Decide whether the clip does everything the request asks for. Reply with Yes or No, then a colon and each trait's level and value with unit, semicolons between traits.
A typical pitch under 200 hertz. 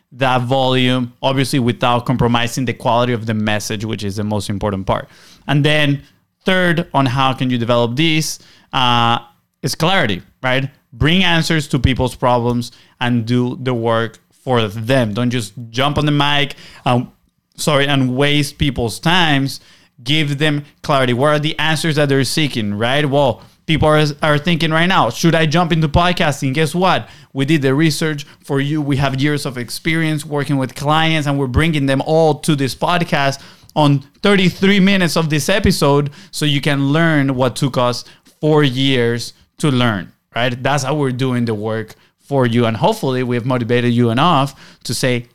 Yes: medium, 140 Hz